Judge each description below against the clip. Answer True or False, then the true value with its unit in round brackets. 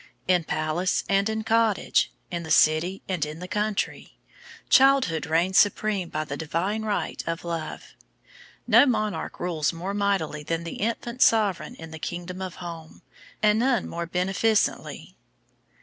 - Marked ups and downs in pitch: False (4.3 semitones)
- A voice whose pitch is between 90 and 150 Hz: False (185 Hz)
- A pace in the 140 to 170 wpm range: True (150 wpm)